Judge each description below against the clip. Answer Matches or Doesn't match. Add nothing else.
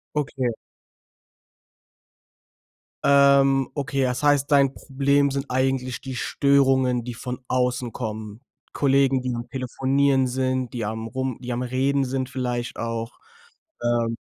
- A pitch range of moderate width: Doesn't match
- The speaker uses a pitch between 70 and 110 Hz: Doesn't match